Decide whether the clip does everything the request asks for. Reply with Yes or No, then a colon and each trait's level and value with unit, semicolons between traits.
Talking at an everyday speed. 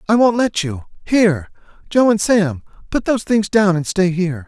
Yes: average, 175 wpm